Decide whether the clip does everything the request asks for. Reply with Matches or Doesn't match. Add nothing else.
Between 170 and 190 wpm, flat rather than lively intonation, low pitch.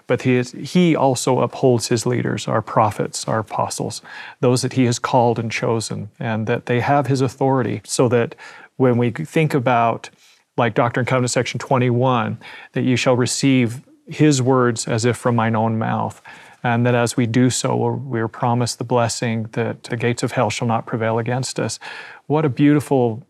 Matches